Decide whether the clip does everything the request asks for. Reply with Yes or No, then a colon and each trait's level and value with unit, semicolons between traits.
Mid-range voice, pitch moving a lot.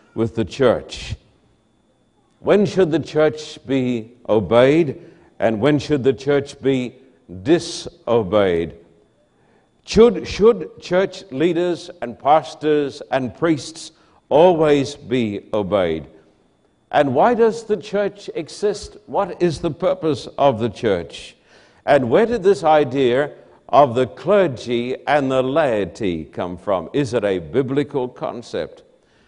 Yes: medium, 150 Hz; wide, 5.8 semitones